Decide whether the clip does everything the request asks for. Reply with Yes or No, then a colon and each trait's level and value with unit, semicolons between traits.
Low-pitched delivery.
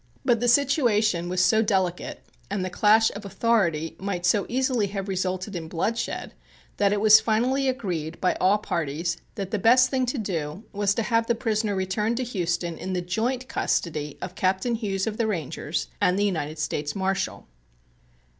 No: high, 200 Hz